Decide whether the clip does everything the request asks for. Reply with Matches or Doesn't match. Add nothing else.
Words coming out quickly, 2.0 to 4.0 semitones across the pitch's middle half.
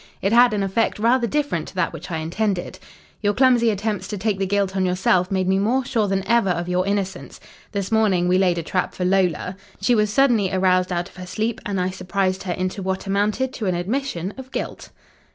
Matches